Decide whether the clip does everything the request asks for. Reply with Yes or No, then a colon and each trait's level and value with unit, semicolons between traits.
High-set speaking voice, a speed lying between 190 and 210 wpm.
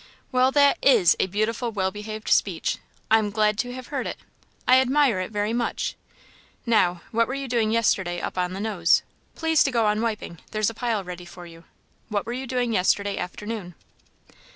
Yes: high, 215 Hz; average, 195 wpm